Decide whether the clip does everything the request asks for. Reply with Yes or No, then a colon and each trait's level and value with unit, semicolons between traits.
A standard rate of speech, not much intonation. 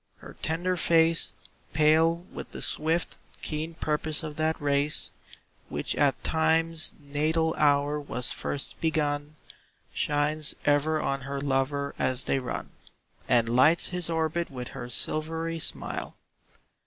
No: slow, 130 wpm; narrow, 2.3 semitones